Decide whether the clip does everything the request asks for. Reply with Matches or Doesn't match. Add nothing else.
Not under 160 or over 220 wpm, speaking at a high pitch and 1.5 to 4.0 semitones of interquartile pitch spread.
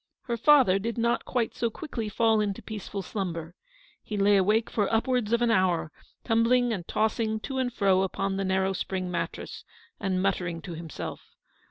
Matches